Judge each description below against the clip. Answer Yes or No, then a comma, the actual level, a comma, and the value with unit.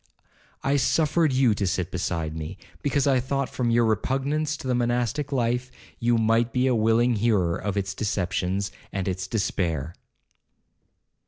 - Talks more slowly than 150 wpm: No, average, 155 wpm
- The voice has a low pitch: Yes, low, 115 Hz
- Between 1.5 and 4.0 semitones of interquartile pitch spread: No, average, 5.1 semitones